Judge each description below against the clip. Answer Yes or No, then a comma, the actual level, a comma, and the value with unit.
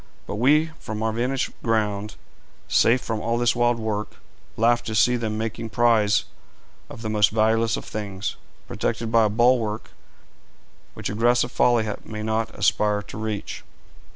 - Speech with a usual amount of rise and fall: No, narrow, 1.8 semitones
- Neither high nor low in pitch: No, low, 110 Hz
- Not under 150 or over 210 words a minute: Yes, average, 155 wpm